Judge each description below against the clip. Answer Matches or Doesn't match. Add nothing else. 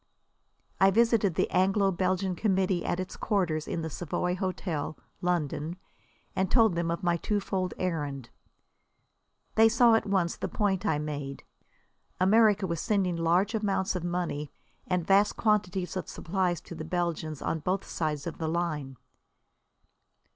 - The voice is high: Doesn't match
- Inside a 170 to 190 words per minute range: Doesn't match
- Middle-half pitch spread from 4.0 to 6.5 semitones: Doesn't match